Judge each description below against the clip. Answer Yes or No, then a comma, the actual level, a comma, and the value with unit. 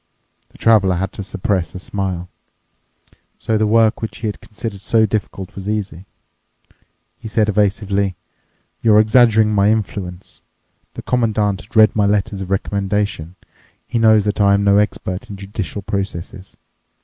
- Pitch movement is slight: Yes, narrow, 1.9 semitones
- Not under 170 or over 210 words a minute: No, average, 150 wpm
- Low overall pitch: Yes, low, 100 Hz